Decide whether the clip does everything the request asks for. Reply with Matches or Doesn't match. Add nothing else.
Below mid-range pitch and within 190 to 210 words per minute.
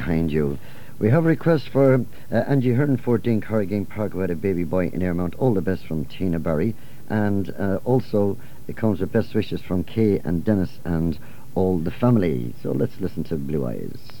Matches